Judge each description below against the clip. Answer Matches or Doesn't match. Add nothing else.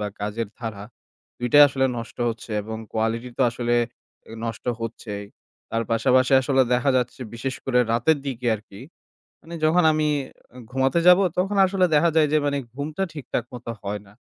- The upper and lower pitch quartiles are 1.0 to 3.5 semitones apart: Doesn't match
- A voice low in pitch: Matches